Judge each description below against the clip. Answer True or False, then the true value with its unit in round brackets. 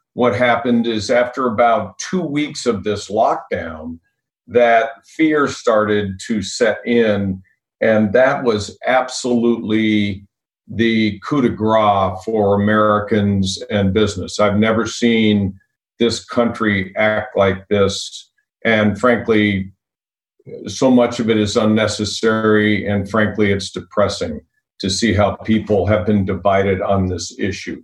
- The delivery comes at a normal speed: False (125 wpm)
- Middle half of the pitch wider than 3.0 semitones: False (2.5 semitones)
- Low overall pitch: True (105 Hz)